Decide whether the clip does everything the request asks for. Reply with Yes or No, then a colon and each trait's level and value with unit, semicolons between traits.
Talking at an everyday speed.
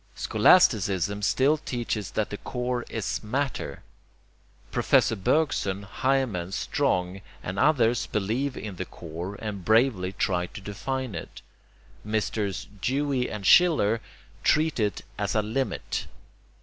No: slow, 120 wpm